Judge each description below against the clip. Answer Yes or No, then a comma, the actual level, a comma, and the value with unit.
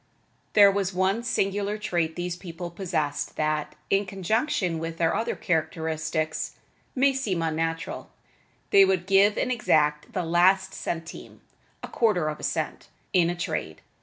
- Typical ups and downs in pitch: Yes, average, 3.4 semitones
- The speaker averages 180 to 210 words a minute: No, average, 145 wpm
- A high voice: No, medium, 175 Hz